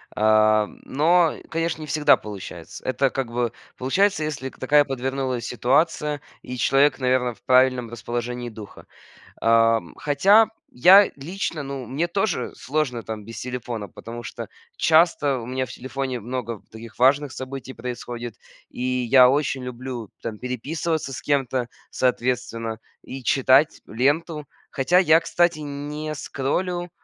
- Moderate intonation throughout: Yes, average, 3.6 semitones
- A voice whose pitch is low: Yes, low, 130 Hz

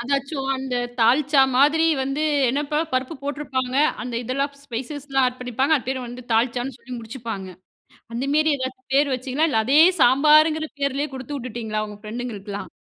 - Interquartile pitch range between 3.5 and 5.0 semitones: No, average, 2.8 semitones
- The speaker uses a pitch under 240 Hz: No, very high, 260 Hz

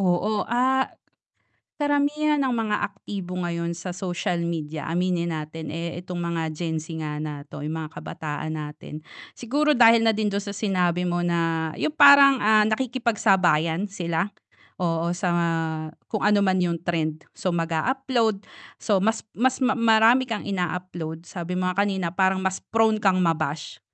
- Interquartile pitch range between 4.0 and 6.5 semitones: Yes, average, 4.7 semitones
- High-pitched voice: No, medium, 180 Hz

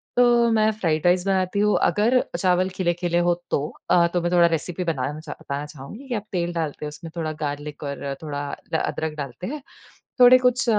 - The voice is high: No, medium, 175 Hz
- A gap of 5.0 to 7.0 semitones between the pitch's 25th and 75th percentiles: Yes, wide, 5.4 semitones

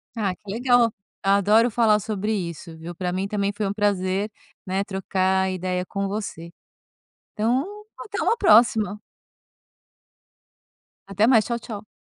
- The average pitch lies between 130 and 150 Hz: No, high, 200 Hz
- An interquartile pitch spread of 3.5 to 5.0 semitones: No, average, 2.7 semitones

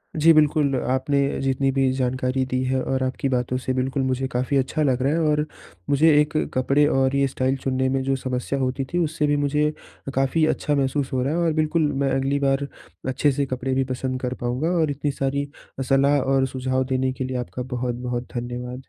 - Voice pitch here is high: No, low, 135 Hz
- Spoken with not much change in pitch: Yes, narrow, 1.6 semitones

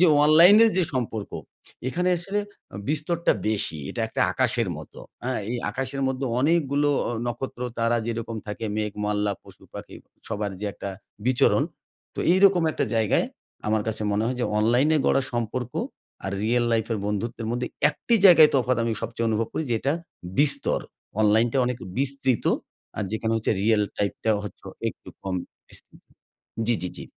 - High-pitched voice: No, low, 120 Hz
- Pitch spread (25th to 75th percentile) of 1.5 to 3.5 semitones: No, average, 4.3 semitones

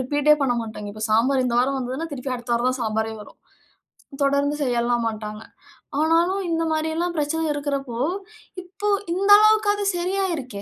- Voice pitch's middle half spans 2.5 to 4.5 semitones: No, wide, 5.6 semitones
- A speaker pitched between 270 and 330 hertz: Yes, very high, 275 Hz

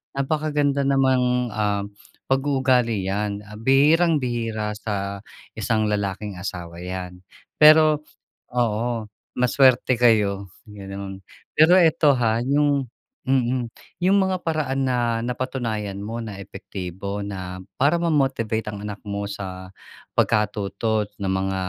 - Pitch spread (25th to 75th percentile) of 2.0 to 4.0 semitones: No, average, 5.0 semitones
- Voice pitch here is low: Yes, low, 115 Hz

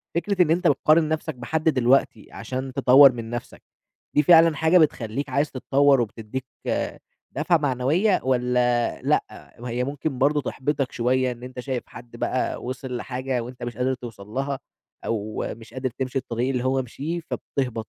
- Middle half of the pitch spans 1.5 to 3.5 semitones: Yes, average, 2.7 semitones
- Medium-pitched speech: No, low, 130 Hz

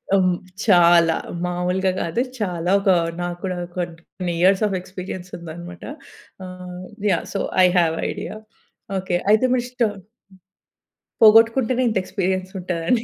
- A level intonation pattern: Yes, narrow, 2.1 semitones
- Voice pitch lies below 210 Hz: Yes, medium, 185 Hz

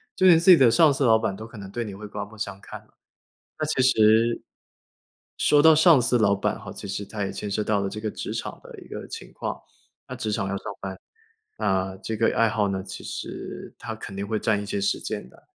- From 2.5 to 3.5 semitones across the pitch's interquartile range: Yes, average, 3.0 semitones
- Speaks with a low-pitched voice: Yes, low, 110 Hz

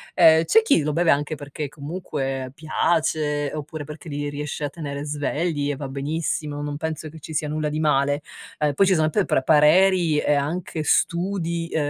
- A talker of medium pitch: Yes, medium, 150 Hz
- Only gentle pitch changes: Yes, narrow, 2.0 semitones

